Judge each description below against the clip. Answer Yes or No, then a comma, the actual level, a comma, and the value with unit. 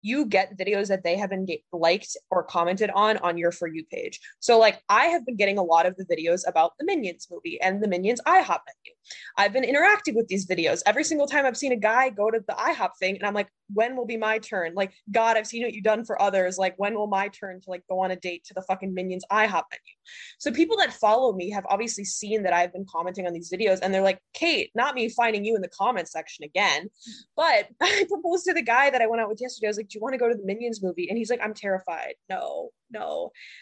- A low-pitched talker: No, high, 215 Hz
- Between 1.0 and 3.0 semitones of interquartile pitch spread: No, average, 5.1 semitones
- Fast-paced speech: Yes, fast, 265 wpm